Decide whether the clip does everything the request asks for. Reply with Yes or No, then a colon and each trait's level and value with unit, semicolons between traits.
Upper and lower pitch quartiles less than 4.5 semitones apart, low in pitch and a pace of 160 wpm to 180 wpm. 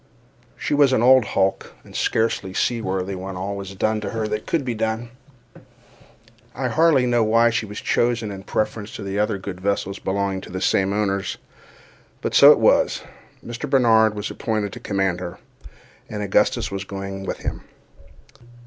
Yes: average, 2.9 semitones; low, 105 Hz; average, 165 wpm